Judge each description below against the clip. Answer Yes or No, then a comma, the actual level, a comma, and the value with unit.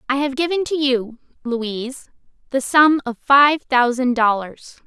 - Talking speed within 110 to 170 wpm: Yes, average, 150 wpm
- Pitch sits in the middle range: No, very high, 260 Hz